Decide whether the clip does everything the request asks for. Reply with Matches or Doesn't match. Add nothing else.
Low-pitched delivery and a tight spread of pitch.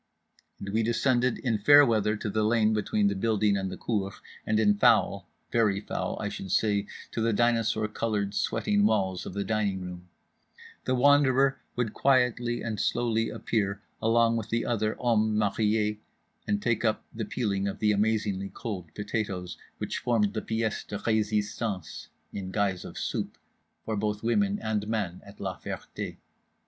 Matches